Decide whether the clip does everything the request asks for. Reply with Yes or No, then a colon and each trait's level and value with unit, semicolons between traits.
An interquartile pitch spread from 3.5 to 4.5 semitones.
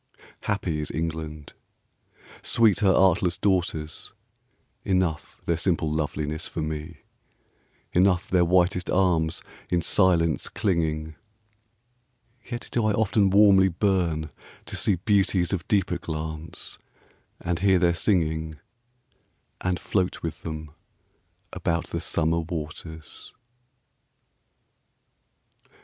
No: average, 3.1 semitones